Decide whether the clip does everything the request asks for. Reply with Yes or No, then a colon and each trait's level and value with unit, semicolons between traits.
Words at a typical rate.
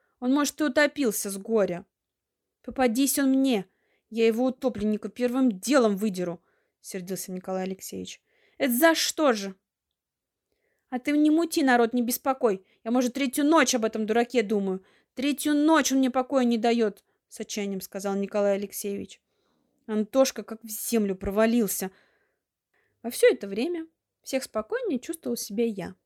Yes: average, 145 wpm